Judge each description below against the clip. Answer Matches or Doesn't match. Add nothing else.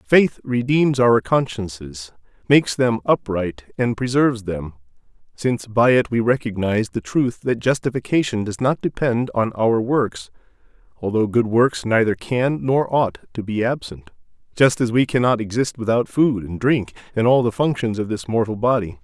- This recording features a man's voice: Matches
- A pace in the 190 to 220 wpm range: Doesn't match